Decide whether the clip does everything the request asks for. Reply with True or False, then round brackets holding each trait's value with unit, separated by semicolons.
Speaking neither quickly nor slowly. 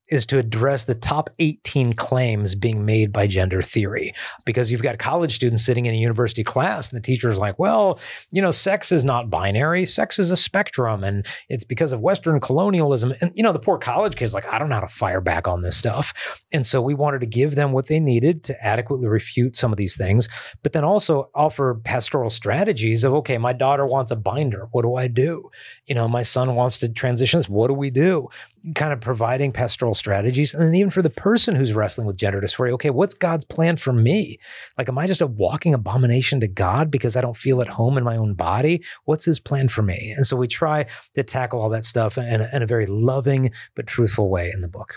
False (230 wpm)